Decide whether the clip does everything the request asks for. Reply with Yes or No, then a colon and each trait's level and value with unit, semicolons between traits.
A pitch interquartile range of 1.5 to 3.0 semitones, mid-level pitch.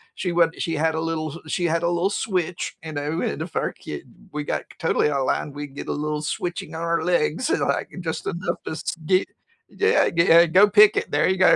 Yes: average, 2.7 semitones; medium, 165 Hz